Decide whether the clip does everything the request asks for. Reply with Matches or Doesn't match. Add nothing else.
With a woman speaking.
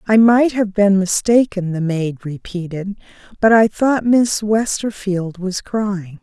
Matches